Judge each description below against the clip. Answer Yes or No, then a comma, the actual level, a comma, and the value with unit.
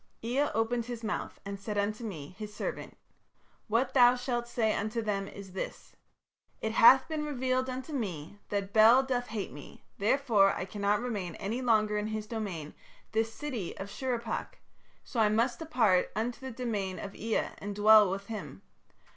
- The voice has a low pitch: No, high, 220 Hz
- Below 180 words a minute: Yes, average, 170 wpm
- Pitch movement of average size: Yes, average, 3.4 semitones